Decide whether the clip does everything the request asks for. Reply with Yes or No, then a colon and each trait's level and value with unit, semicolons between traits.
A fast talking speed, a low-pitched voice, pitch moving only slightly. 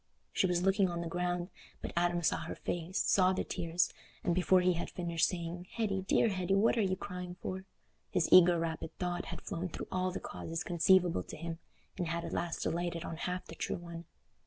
No: fast, 210 wpm; medium, 175 Hz; narrow, 1.5 semitones